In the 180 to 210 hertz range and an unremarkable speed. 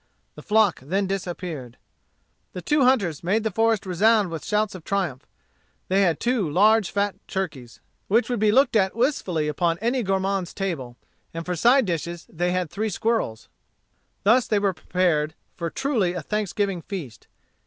Yes: high, 190 Hz; average, 165 wpm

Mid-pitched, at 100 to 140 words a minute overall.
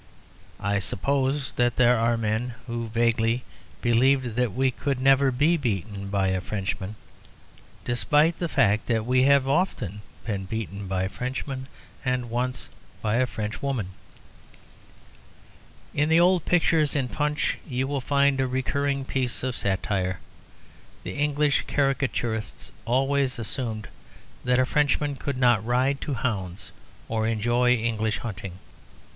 No: low, 125 Hz; slow, 135 wpm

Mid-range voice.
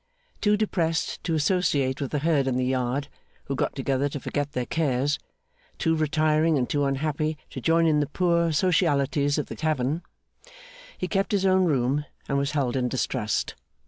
Yes: medium, 150 Hz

